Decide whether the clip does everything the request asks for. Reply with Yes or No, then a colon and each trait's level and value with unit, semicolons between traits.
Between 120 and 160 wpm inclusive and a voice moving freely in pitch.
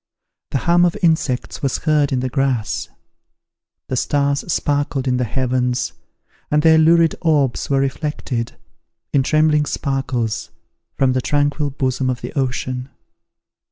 No: slow, 135 wpm; average, 2.8 semitones